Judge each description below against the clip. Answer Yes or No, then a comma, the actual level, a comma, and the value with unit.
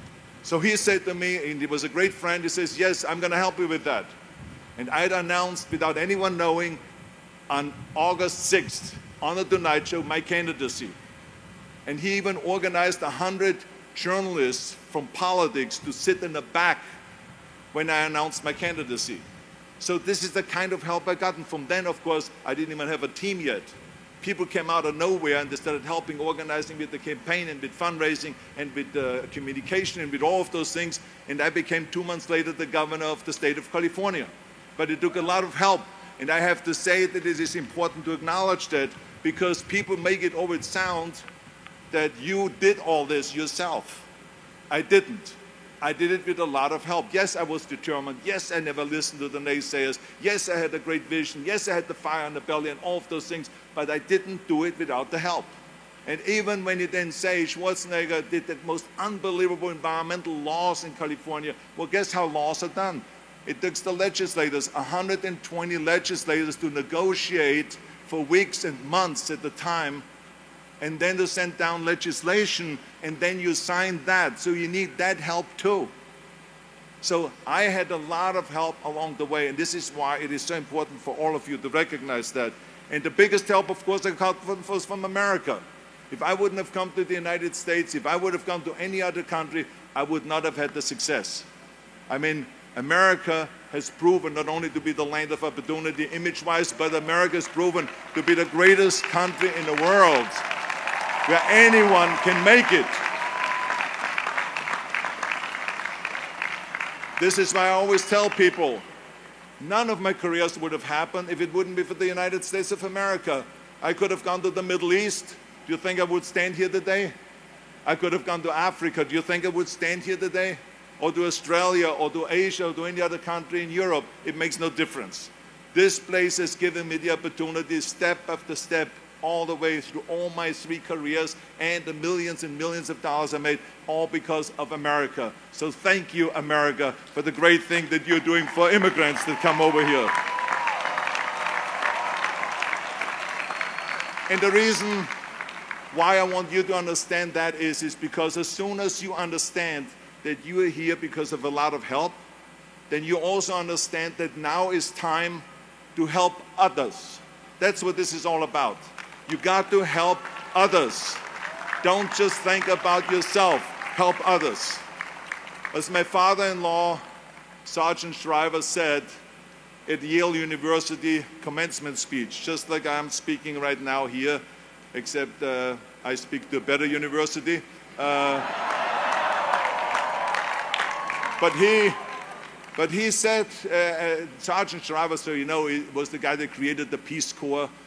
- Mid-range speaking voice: Yes, medium, 170 Hz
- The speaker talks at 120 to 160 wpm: No, average, 180 wpm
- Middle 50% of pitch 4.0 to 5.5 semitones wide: No, average, 2.8 semitones